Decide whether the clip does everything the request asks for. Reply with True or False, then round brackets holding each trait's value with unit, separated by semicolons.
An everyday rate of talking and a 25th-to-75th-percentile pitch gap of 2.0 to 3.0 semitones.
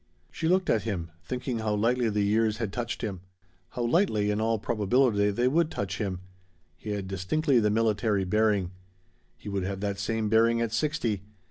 True (185 wpm; 2.7 semitones)